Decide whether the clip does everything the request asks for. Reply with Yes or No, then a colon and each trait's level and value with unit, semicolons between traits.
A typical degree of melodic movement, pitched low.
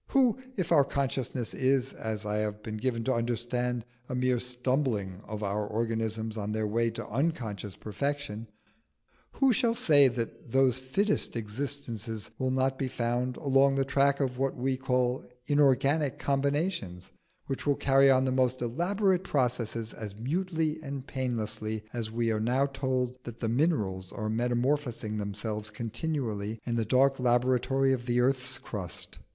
Yes: average, 3.5 semitones; low, 125 Hz